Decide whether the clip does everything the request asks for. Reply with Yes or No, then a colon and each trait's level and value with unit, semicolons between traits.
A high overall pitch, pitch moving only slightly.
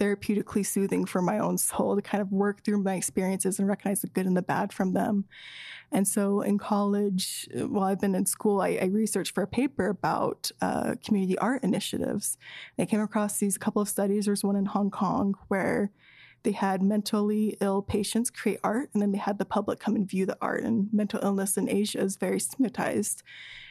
Yes: high, 205 Hz; narrow, 1.3 semitones